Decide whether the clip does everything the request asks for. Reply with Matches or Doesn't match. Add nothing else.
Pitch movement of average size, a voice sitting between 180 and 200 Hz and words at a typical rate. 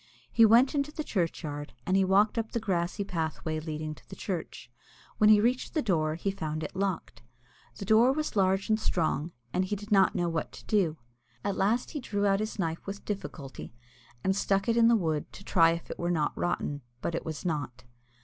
Doesn't match